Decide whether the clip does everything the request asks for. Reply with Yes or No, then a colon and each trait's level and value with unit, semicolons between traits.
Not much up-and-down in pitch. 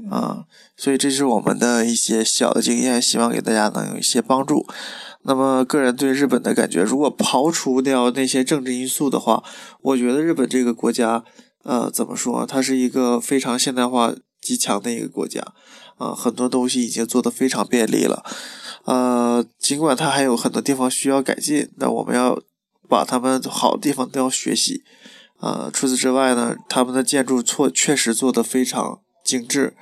Yes: narrow, 2.1 semitones